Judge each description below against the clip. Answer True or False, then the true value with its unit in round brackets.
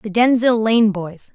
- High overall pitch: True (215 Hz)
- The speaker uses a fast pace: False (180 wpm)